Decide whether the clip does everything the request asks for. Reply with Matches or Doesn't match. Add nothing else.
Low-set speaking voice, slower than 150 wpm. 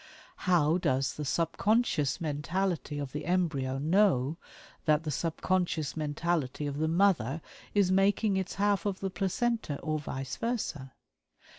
Doesn't match